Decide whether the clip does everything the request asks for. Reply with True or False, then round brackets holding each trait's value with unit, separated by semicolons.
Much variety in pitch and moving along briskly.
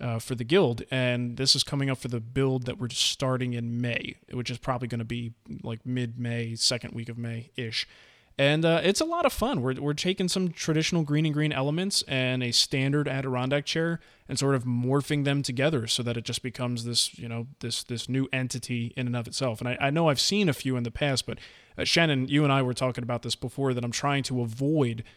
False (2.9 semitones; 240 wpm)